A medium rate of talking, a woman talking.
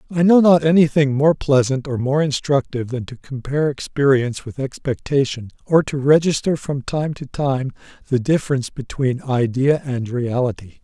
No: average, 160 wpm; male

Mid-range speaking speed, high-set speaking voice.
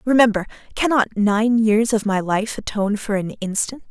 Yes: average, 170 wpm; high, 215 Hz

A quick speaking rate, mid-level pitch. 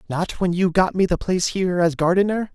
Yes: fast, 235 wpm; medium, 180 Hz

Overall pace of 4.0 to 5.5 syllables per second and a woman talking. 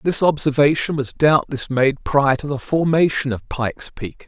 No: 4.6 syllables/s; male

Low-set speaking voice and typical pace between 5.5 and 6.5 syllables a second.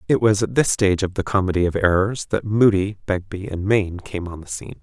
Yes: very low, 95 Hz; 5.9 syllables/s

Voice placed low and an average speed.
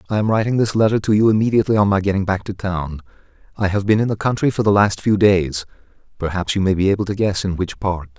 No: low, 100 Hz; fast, 255 wpm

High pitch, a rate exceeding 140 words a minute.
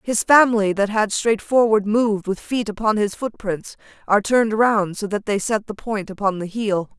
Yes: high, 210 Hz; fast, 205 wpm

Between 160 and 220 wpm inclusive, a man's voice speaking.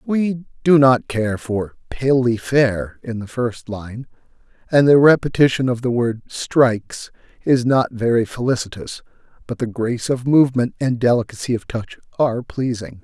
No: average, 150 wpm; male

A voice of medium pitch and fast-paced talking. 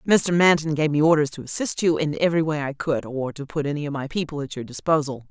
Yes: medium, 150 Hz; fast, 260 wpm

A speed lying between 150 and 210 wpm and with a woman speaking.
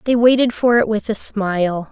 No: fast, 220 wpm; female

